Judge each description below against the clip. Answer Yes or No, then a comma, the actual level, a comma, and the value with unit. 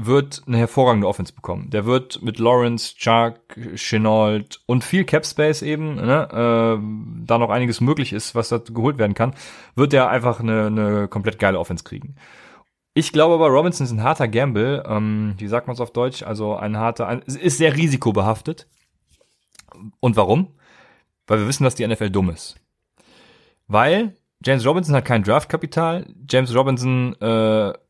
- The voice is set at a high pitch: No, low, 120 Hz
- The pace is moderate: Yes, average, 170 wpm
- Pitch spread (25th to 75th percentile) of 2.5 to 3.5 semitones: No, average, 4.3 semitones